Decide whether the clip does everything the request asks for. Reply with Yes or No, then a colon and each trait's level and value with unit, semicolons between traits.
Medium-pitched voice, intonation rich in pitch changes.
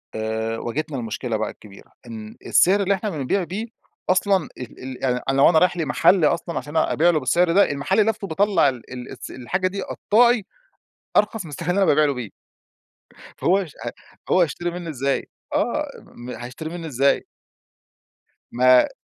Yes: medium, 160 Hz; wide, 6.5 semitones